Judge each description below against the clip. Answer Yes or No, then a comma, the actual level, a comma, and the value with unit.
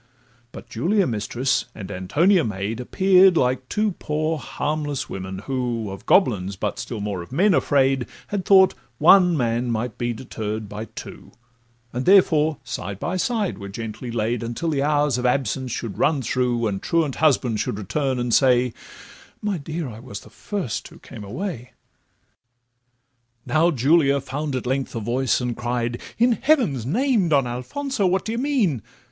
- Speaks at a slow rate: No, average, 165 wpm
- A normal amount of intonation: No, wide, 6.2 semitones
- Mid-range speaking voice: No, low, 130 Hz